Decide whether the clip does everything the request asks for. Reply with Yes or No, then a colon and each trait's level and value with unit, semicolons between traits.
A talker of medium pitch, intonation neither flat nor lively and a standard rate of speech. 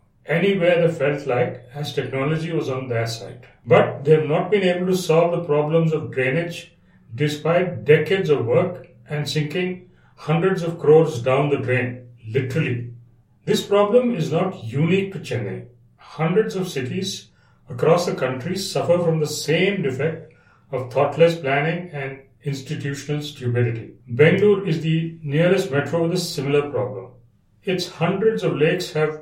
Yes: medium, 155 Hz; average, 4.6 semitones; average, 150 wpm